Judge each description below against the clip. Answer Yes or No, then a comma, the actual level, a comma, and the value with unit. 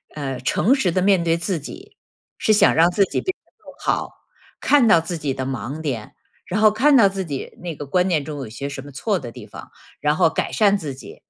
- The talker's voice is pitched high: No, medium, 165 Hz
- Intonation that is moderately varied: No, wide, 6.0 semitones